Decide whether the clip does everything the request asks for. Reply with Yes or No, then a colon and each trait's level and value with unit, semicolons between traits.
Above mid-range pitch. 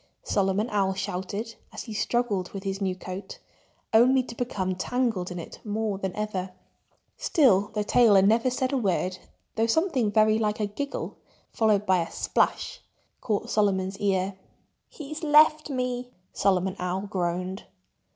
Yes: high, 205 Hz